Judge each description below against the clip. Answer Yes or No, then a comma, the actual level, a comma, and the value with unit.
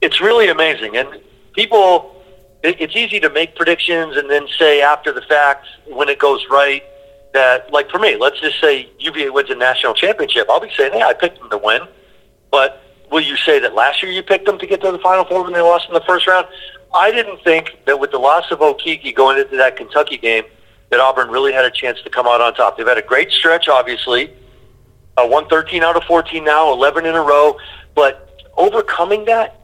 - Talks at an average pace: No, fast, 220 wpm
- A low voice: No, medium, 160 Hz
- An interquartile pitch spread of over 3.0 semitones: Yes, average, 5.1 semitones